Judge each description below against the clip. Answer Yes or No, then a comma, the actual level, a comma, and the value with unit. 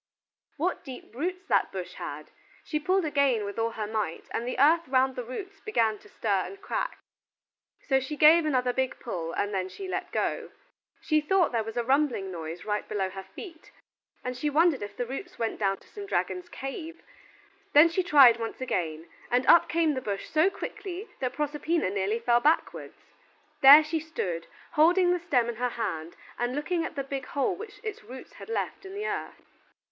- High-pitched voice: Yes, very high, 270 Hz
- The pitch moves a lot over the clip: Yes, wide, 6.7 semitones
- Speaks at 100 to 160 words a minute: No, average, 195 wpm